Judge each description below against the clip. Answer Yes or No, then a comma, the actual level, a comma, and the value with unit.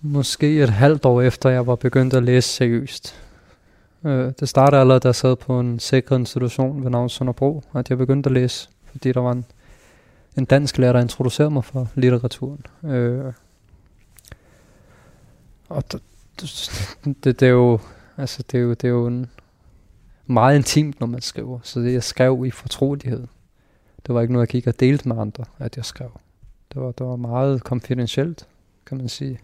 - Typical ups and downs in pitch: No, narrow, 1.8 semitones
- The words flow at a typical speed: Yes, average, 185 wpm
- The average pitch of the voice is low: Yes, low, 125 Hz